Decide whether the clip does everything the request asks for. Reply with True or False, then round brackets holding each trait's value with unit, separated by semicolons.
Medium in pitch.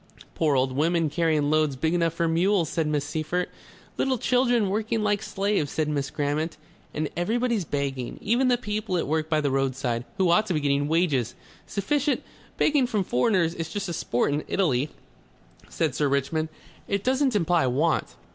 True (165 Hz)